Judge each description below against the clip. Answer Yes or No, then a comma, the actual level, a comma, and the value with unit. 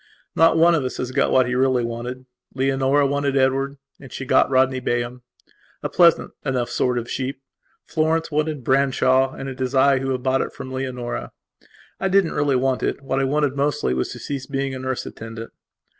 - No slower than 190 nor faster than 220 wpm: Yes, fast, 205 wpm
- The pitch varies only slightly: Yes, narrow, 1.6 semitones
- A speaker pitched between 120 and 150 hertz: Yes, low, 135 Hz